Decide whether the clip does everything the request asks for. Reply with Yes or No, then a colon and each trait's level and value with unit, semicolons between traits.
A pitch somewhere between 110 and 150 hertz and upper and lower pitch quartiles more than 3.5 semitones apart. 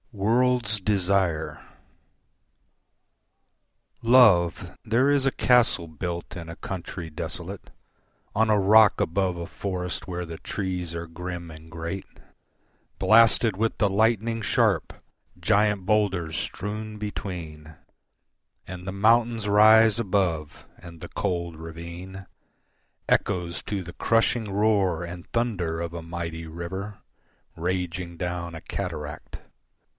No: very low, 90 Hz; average, 3.9 semitones